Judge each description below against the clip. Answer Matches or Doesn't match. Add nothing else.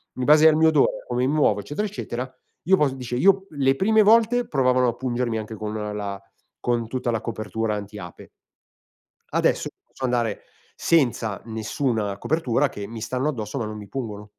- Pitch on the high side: Doesn't match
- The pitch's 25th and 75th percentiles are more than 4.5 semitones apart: Matches